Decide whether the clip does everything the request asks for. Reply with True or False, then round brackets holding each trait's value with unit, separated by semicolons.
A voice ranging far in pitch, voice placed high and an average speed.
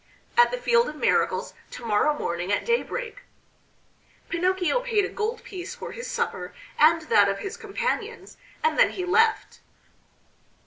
True (7.6 semitones; 415 Hz; 150 wpm)